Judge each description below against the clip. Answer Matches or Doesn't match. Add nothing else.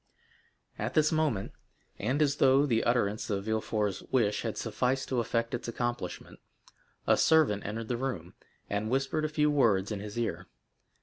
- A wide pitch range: Doesn't match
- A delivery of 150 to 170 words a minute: Matches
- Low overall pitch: Matches